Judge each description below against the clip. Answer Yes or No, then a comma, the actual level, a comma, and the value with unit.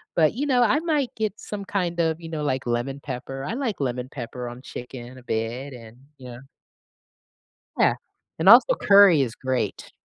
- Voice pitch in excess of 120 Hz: Yes, medium, 140 Hz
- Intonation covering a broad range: Yes, wide, 8.3 semitones